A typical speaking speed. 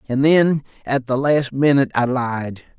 Yes: average, 170 wpm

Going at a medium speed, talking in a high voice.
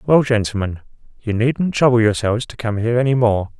No: average, 185 wpm; low, 115 Hz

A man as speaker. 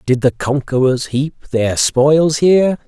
Yes: male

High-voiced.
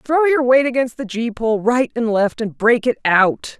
Yes: high, 240 Hz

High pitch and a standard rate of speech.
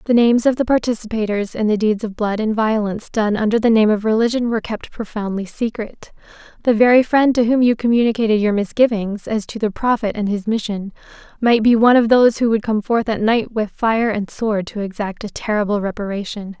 No: high, 220 Hz; fast, 210 wpm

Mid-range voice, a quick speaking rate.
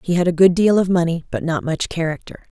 Yes: medium, 170 Hz; fast, 255 wpm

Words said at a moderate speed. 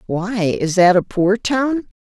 Yes: average, 175 wpm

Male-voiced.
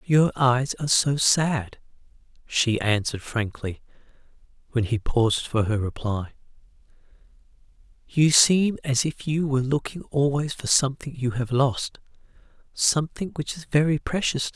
Yes: male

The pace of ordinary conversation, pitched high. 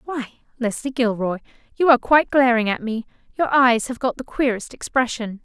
Yes: average, 175 wpm; high, 245 Hz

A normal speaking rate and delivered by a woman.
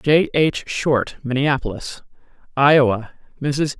No: slow, 95 wpm; female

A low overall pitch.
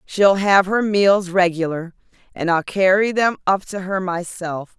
No: medium, 185 Hz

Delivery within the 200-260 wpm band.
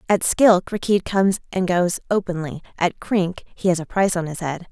Yes: fast, 205 wpm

